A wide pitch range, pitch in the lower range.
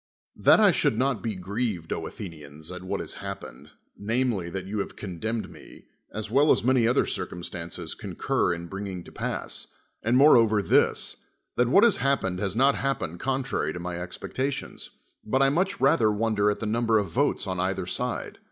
Yes: wide, 5.7 semitones; low, 105 Hz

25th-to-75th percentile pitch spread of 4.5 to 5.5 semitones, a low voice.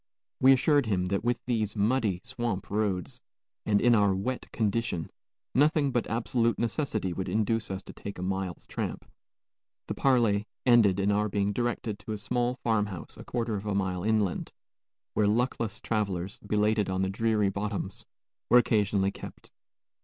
No: average, 3.2 semitones; low, 105 Hz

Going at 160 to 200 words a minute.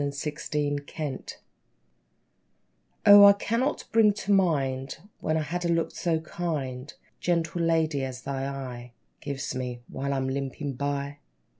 No: average, 140 wpm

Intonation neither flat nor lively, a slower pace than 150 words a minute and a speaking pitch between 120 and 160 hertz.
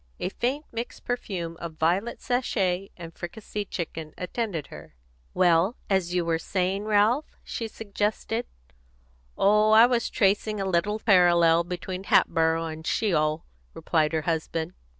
No: average, 4.4 semitones; average, 140 wpm; medium, 185 Hz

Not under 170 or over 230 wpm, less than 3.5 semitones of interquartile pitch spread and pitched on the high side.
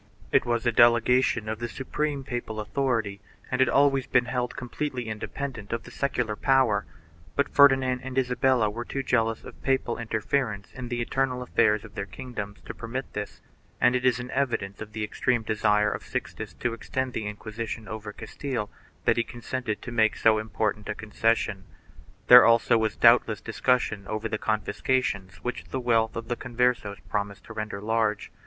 No: average, 180 wpm; average, 2.8 semitones; low, 115 Hz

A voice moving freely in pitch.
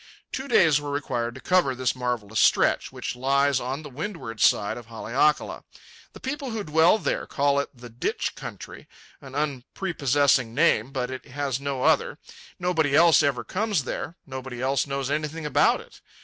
No: average, 3.6 semitones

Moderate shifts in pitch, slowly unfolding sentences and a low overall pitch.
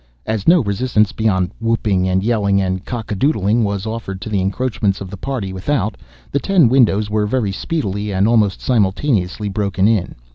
No: average, 3.1 semitones; average, 180 wpm; low, 105 Hz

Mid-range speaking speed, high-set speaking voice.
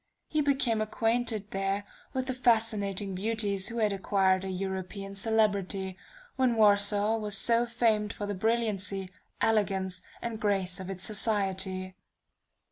No: slow, 130 wpm; high, 205 Hz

